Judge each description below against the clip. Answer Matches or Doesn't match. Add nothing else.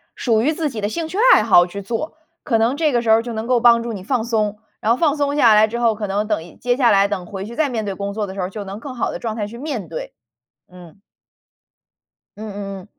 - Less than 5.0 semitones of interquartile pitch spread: Matches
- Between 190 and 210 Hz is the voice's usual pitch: Doesn't match